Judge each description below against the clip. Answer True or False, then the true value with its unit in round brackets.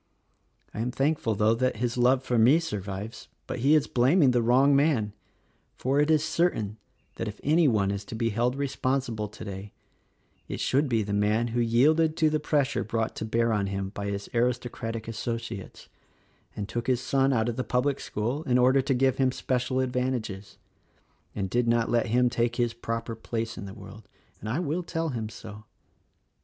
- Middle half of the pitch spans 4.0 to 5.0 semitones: False (3.3 semitones)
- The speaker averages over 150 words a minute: True (195 wpm)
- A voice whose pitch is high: False (120 Hz)